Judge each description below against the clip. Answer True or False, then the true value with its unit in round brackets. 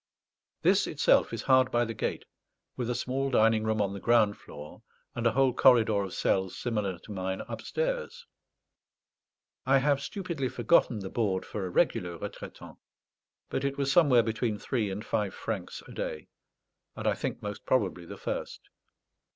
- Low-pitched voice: True (115 Hz)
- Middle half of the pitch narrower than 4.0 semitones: False (4.6 semitones)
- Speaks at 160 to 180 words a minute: True (165 wpm)